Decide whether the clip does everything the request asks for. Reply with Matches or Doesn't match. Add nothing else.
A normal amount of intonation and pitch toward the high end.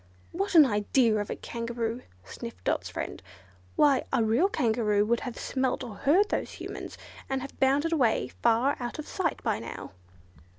Matches